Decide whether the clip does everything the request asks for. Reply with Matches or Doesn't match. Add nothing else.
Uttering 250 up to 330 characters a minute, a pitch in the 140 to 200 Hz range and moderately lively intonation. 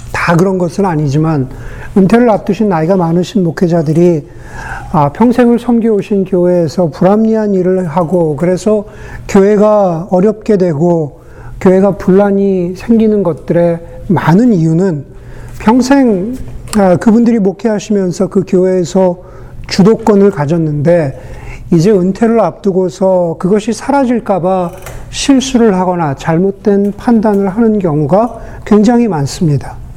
Matches